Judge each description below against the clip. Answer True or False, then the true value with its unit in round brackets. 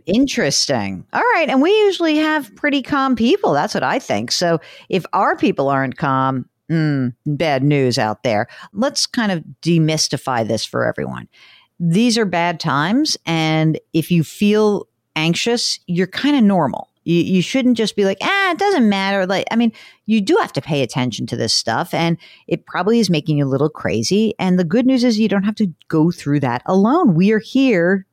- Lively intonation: True (7.4 semitones)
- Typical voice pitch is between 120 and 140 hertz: False (180 Hz)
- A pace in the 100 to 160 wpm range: False (195 wpm)